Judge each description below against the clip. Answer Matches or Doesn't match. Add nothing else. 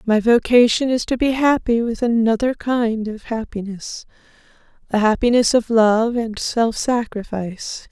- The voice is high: Matches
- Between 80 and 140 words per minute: Matches